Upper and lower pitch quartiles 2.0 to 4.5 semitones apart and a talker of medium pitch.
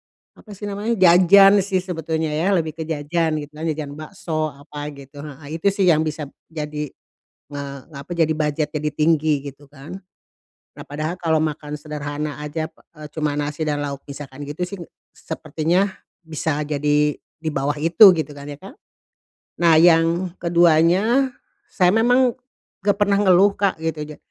Yes: average, 3.2 semitones; medium, 155 Hz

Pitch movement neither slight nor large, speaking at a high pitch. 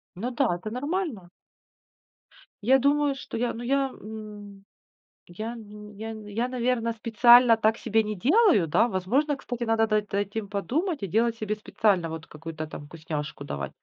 Yes: average, 3.6 semitones; high, 220 Hz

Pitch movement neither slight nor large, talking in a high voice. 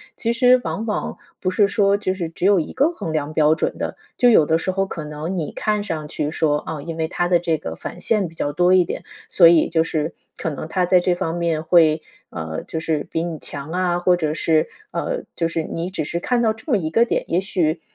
No: average, 3.3 semitones; medium, 170 Hz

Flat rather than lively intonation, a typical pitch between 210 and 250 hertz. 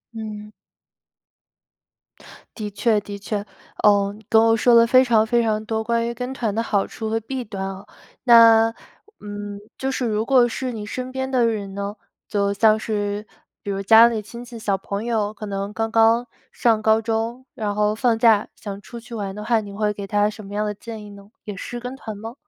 Yes: narrow, 2.2 semitones; high, 220 Hz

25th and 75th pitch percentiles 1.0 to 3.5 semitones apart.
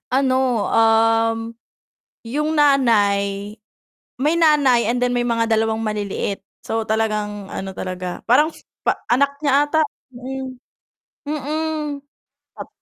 No: average, 4.6 semitones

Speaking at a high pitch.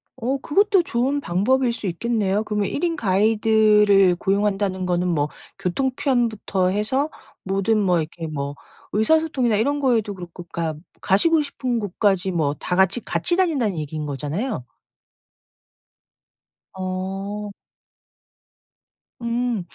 Yes: high, 205 Hz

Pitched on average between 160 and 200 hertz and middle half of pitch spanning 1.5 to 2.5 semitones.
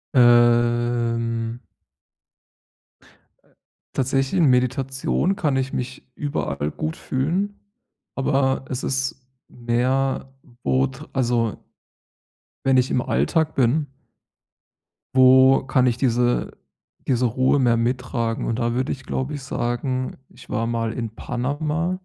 No: low, 130 Hz; narrow, 2.1 semitones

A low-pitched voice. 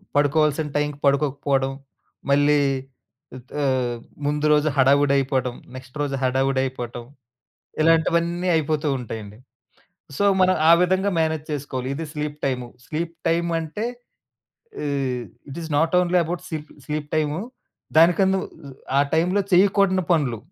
No: medium, 150 Hz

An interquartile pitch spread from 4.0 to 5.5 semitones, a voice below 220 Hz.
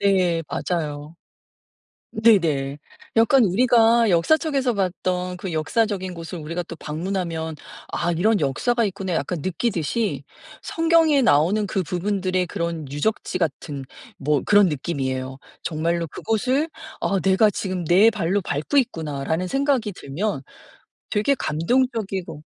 Yes: average, 5.2 semitones; medium, 185 Hz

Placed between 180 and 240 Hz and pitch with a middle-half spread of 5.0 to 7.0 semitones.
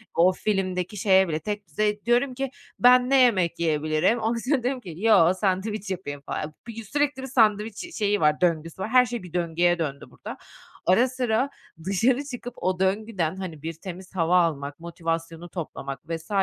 Yes: high, 190 Hz; wide, 5.4 semitones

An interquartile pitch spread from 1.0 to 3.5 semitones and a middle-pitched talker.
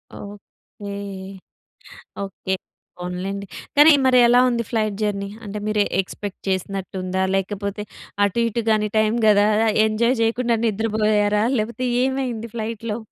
No: narrow, 2.5 semitones; high, 210 Hz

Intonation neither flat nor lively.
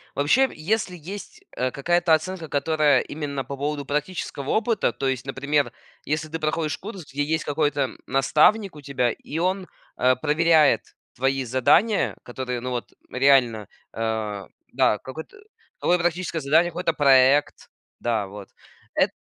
Yes: average, 4.0 semitones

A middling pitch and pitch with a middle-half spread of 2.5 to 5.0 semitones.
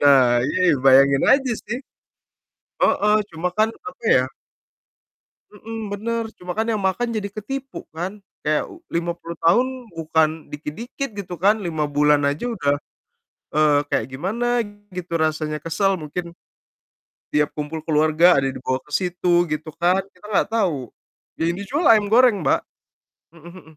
No: medium, 175 Hz; wide, 5.6 semitones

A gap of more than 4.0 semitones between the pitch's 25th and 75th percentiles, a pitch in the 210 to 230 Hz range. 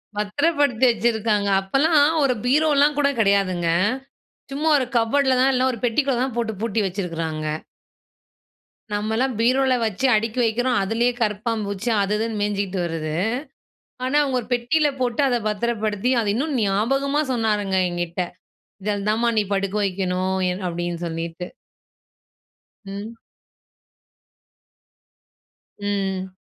Yes: average, 4.7 semitones; high, 220 Hz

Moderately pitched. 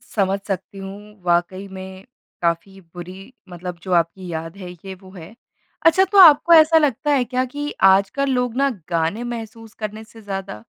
No: high, 195 Hz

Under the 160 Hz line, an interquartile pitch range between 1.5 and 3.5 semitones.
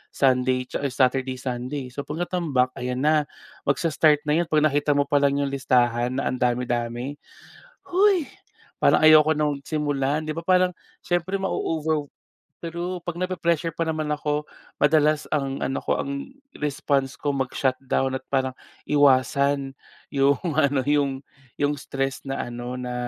Yes: medium, 140 Hz; average, 2.8 semitones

